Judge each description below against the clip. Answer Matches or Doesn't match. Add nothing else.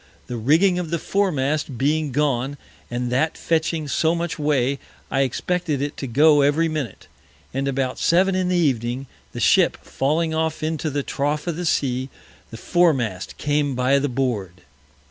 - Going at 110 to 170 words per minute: Matches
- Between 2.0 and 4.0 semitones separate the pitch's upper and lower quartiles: Matches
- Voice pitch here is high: Doesn't match